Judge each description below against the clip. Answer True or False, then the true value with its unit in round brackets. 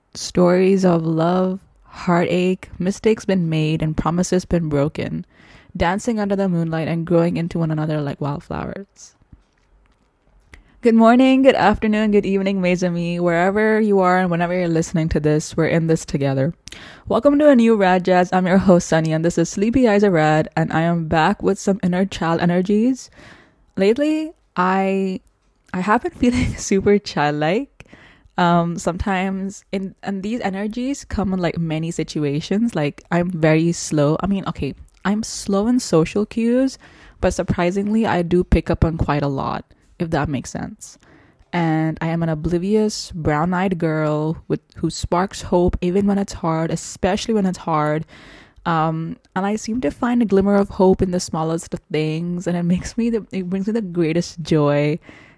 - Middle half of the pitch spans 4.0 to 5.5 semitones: False (3.6 semitones)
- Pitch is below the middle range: False (180 Hz)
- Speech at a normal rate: True (170 wpm)